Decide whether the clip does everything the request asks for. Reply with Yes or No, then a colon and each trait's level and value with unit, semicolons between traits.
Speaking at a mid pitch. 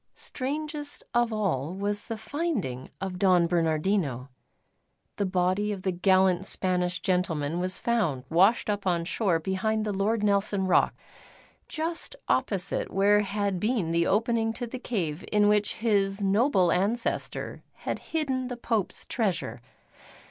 No: high, 200 Hz